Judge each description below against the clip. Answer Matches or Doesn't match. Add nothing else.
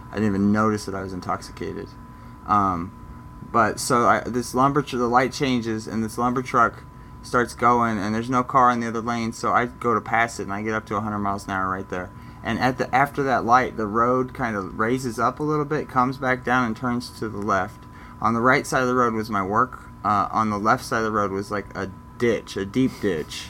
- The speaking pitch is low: Matches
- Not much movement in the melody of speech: Doesn't match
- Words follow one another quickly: Matches